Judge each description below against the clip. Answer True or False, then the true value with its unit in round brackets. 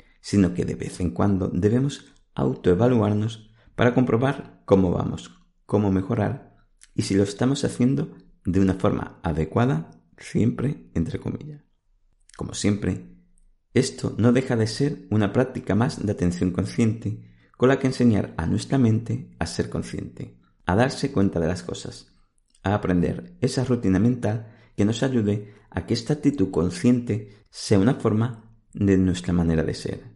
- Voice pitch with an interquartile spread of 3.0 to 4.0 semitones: False (4.8 semitones)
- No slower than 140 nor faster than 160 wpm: True (150 wpm)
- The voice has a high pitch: False (105 Hz)